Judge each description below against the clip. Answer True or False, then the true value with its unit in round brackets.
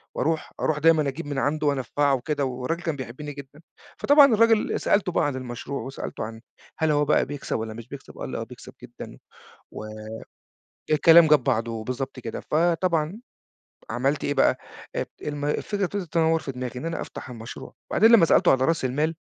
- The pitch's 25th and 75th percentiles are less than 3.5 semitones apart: False (4.1 semitones)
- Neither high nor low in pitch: True (145 Hz)